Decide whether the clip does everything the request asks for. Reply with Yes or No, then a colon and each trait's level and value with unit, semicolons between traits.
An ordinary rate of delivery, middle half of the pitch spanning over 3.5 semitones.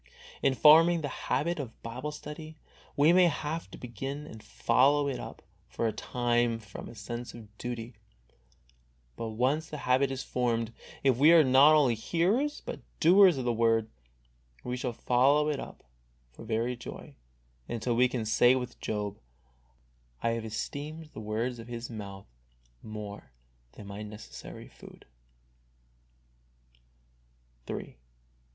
Yes: average, 145 wpm; average, 4.7 semitones